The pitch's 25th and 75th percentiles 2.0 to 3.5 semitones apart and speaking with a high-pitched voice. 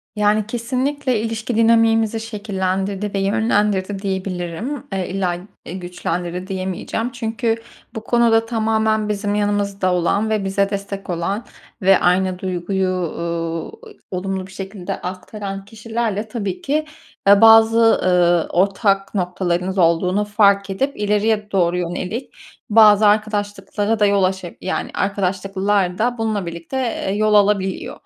Yes: average, 2.8 semitones; high, 200 Hz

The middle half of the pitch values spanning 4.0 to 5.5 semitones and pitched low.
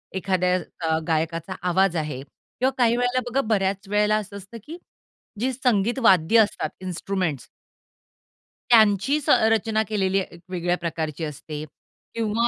No: average, 4.7 semitones; high, 195 Hz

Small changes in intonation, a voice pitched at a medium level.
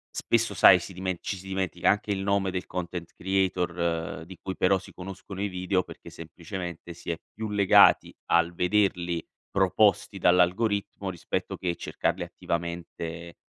No: narrow, 2.1 semitones; very low, 90 Hz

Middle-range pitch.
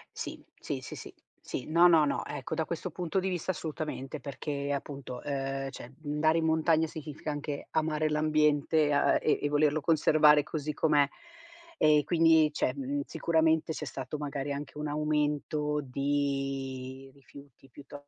Yes: medium, 150 Hz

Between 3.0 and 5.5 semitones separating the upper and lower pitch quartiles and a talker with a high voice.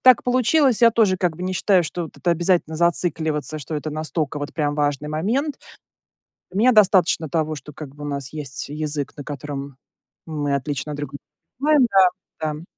No: average, 4.2 semitones; medium, 155 Hz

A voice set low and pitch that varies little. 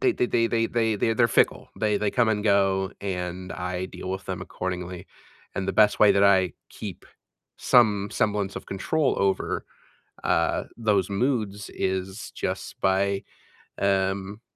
Yes: low, 100 Hz; narrow, 2.3 semitones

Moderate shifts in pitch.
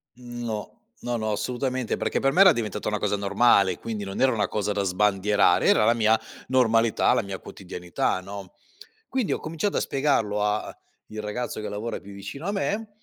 Yes: average, 3.6 semitones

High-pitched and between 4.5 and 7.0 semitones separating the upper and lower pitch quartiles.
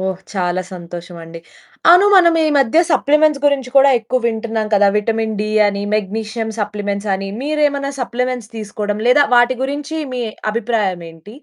Yes: high, 225 Hz; average, 5.1 semitones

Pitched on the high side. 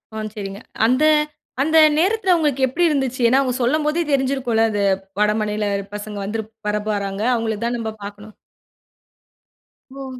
Yes: high, 235 Hz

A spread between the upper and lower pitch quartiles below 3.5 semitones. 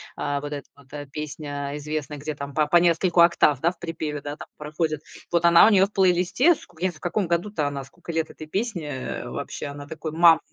Yes: average, 3.0 semitones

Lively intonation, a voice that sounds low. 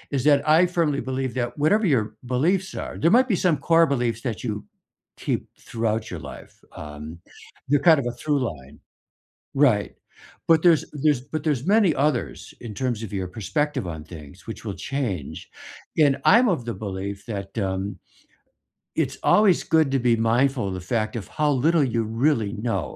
Yes: wide, 6.8 semitones; low, 130 Hz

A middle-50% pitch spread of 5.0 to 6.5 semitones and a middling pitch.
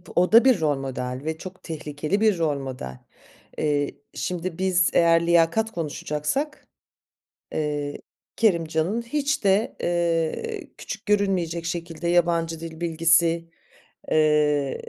No: average, 3.5 semitones; medium, 170 Hz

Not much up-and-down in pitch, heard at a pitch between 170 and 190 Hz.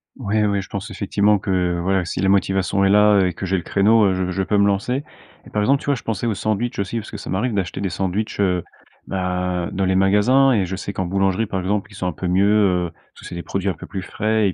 No: narrow, 2.1 semitones; low, 100 Hz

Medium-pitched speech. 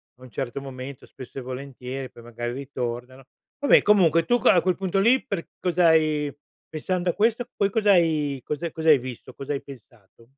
Yes: medium, 145 Hz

